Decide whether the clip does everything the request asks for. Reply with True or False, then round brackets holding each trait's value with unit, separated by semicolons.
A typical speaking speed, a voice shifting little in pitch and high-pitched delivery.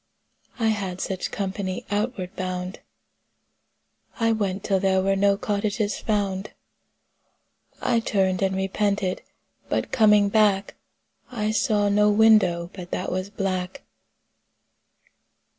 False (110 wpm; 2.0 semitones; 200 Hz)